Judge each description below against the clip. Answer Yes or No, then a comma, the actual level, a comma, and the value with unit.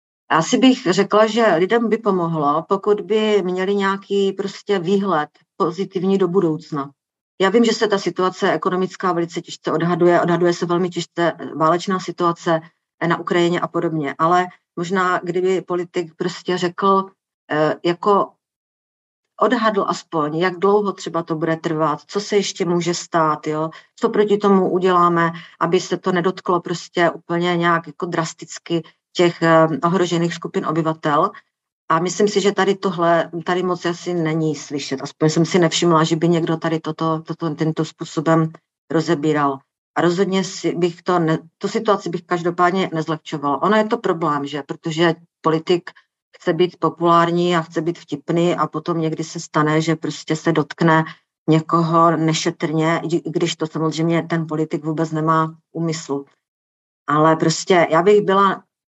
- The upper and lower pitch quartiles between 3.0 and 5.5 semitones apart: No, narrow, 2.5 semitones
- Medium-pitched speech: Yes, medium, 170 Hz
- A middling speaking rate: Yes, average, 150 wpm